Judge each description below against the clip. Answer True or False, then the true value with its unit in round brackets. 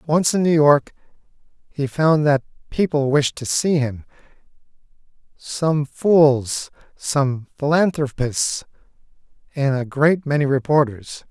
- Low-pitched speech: False (145 Hz)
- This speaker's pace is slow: True (110 wpm)